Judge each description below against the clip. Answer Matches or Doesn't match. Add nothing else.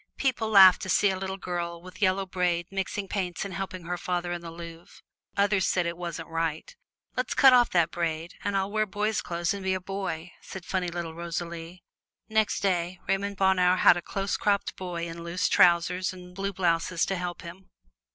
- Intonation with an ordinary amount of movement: Doesn't match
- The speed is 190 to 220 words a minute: Matches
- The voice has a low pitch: Doesn't match